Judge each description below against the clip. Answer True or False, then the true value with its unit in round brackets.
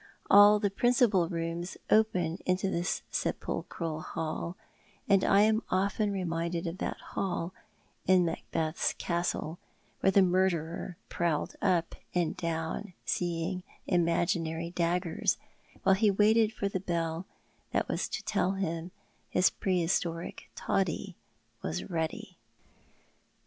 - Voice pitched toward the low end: False (180 Hz)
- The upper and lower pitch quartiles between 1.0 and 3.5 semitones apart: True (2.6 semitones)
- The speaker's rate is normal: False (120 wpm)